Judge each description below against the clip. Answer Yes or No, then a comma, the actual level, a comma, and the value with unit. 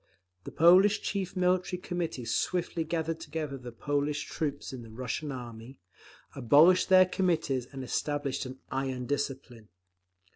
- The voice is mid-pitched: Yes, medium, 145 Hz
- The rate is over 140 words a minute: No, slow, 135 wpm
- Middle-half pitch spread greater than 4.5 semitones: Yes, average, 5.2 semitones